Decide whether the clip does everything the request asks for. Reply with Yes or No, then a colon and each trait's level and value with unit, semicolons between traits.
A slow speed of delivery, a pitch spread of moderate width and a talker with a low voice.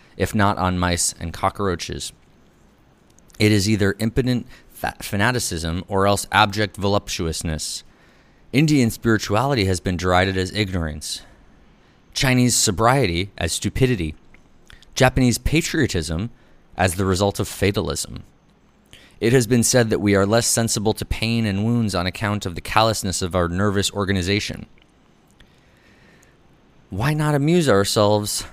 Yes: slow, 125 wpm; average, 3.6 semitones; low, 100 Hz